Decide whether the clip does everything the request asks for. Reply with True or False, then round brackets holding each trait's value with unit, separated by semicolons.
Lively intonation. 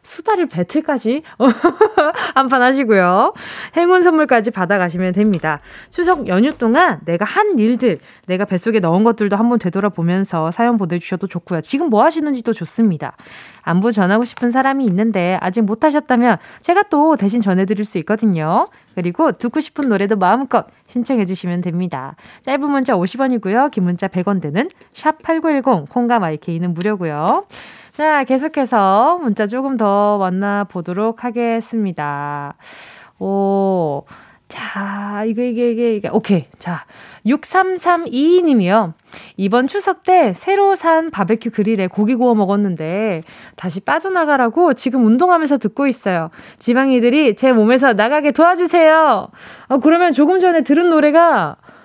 True (7.2 semitones)